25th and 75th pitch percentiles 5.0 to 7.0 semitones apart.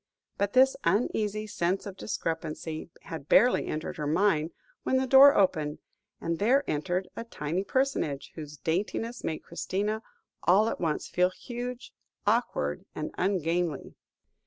Yes: wide, 5.4 semitones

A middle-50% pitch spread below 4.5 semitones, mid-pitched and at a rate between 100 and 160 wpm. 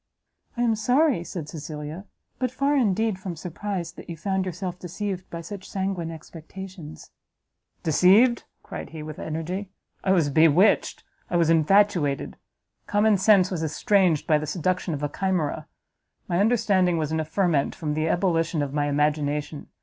Yes: average, 3.9 semitones; medium, 175 Hz; average, 155 wpm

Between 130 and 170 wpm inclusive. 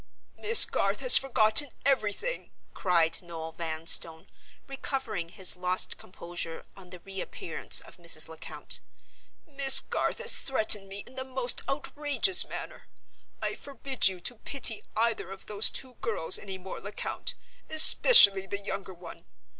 Yes: average, 140 wpm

